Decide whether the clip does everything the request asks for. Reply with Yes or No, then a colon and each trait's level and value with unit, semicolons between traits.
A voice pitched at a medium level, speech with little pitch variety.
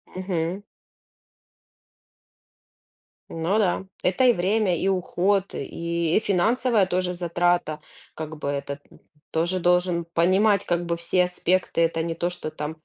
Yes: medium, 175 Hz; narrow, 2.0 semitones